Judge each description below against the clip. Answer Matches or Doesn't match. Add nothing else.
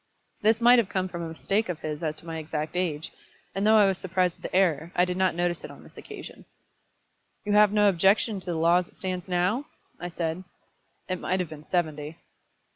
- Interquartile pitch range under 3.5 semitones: Matches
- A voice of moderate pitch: Matches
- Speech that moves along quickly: Matches